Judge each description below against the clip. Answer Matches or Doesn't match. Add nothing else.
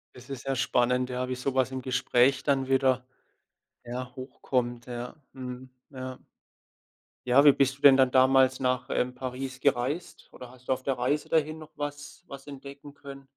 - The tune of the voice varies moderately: Doesn't match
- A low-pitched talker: Matches